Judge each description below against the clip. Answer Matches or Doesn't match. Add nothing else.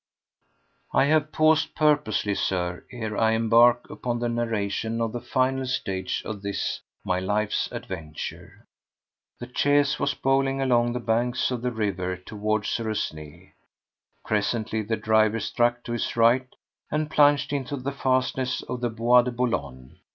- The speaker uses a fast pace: Doesn't match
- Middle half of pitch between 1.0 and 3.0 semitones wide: Doesn't match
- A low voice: Matches